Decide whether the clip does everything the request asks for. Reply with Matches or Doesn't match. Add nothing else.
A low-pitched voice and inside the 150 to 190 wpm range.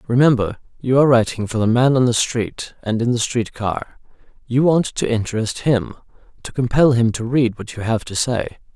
Doesn't match